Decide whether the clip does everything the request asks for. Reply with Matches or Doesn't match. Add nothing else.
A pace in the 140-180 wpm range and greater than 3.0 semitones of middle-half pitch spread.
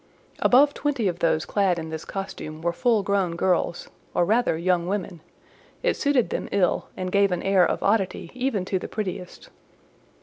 Matches